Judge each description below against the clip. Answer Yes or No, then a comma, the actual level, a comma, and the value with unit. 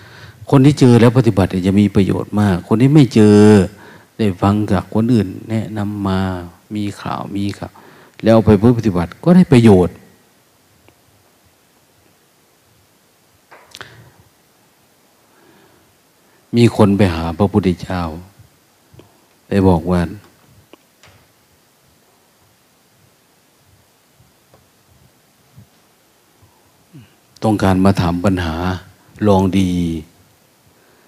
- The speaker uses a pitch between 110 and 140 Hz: No, low, 100 Hz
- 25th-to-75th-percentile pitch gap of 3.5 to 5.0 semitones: No, average, 3.1 semitones